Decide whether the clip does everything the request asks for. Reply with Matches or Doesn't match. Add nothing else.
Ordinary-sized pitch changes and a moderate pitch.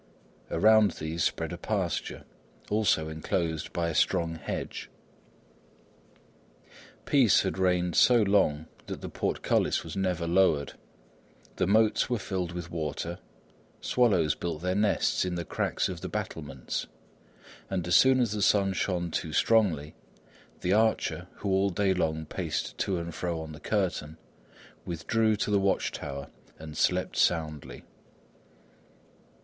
Doesn't match